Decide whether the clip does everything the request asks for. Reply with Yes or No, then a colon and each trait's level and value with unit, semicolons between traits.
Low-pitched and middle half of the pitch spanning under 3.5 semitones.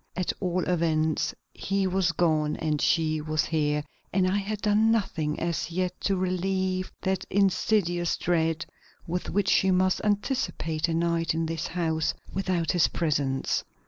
No: medium, 175 Hz; average, 2.9 semitones